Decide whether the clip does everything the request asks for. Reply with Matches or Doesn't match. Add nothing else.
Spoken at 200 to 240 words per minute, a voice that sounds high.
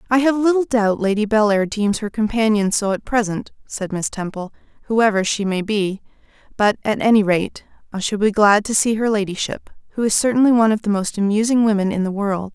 Matches